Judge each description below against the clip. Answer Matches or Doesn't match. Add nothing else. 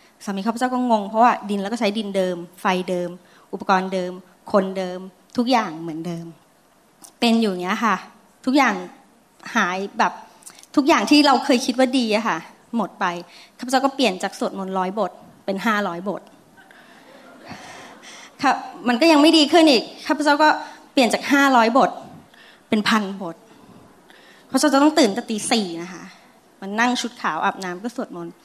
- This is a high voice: Matches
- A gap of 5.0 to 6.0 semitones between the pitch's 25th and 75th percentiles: Matches